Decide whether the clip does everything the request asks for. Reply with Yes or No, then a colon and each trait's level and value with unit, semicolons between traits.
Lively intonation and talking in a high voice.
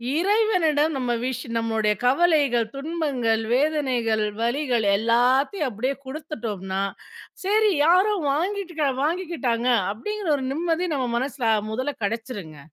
Yes: wide, 5.9 semitones; very high, 275 Hz